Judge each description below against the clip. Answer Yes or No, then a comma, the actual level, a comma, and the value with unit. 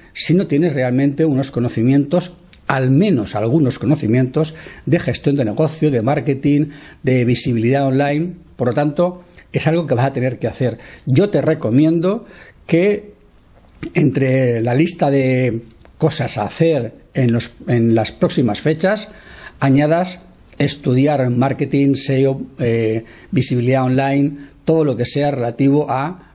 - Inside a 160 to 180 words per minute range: No, average, 135 wpm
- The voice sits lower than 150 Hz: Yes, medium, 140 Hz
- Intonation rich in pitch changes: No, average, 4.0 semitones